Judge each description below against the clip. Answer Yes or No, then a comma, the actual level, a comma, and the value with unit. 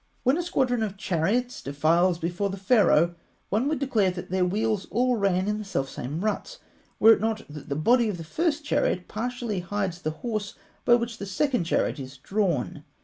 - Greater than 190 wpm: Yes, average, 200 wpm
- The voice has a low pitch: No, high, 200 Hz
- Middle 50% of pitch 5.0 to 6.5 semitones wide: Yes, wide, 5.5 semitones